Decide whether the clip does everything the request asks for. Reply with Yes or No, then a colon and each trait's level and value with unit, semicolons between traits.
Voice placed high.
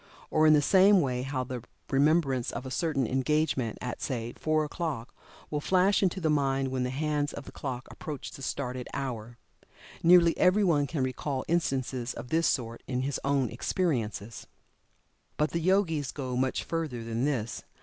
No: medium, 140 Hz